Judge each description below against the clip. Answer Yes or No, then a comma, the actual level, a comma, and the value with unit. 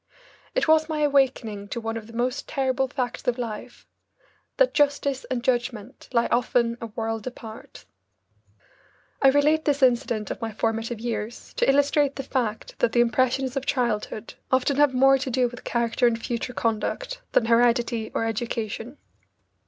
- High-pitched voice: Yes, high, 245 Hz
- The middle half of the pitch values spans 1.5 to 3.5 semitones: Yes, average, 2.9 semitones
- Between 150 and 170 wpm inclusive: Yes, average, 160 wpm